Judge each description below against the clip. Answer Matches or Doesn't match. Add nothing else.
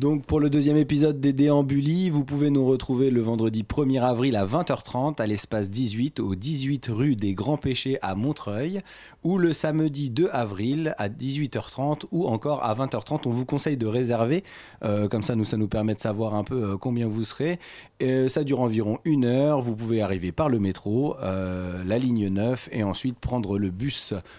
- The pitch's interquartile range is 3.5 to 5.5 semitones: Matches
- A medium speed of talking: Matches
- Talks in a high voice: Doesn't match